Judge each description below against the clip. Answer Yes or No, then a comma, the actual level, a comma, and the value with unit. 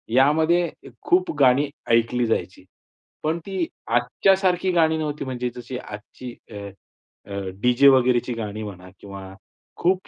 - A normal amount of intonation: No, wide, 6.2 semitones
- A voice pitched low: Yes, low, 125 Hz